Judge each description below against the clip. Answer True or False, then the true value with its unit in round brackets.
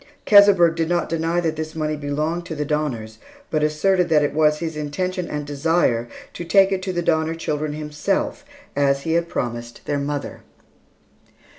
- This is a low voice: False (155 Hz)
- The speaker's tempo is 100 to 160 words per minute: False (175 wpm)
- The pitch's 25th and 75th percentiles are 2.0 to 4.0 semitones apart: True (2.6 semitones)